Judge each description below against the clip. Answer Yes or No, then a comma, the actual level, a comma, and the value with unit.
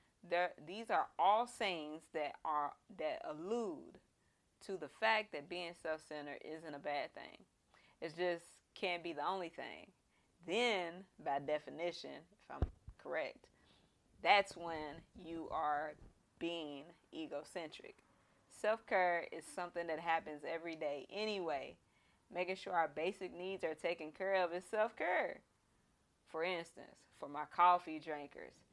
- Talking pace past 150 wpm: No, average, 140 wpm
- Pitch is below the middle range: No, medium, 170 Hz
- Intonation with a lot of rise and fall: No, average, 3.2 semitones